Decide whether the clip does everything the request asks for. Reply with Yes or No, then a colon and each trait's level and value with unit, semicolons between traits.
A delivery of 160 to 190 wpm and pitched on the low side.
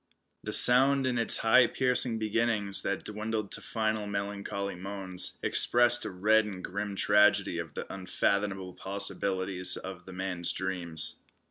No: average, 140 wpm; low, 100 Hz